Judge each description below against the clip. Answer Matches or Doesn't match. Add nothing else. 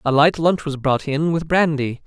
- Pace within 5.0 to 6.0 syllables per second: Doesn't match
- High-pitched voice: Doesn't match